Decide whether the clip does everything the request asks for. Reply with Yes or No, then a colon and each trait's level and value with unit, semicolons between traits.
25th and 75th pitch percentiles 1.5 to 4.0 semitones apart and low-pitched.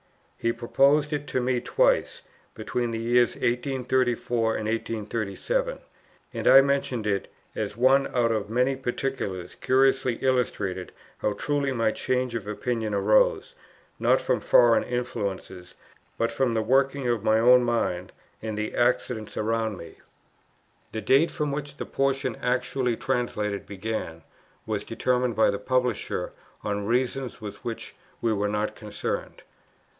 Yes: average, 3.3 semitones; low, 120 Hz